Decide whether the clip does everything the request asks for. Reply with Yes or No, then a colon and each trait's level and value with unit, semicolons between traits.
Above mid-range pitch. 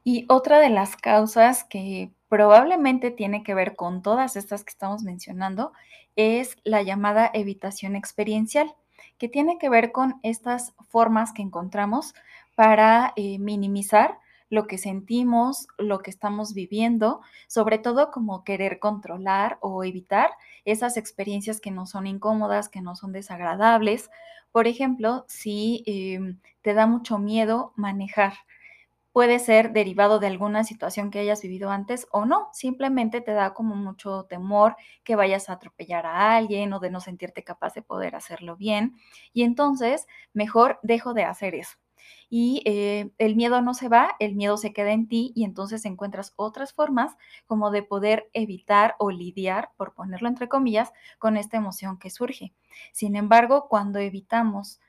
Yes: high, 215 Hz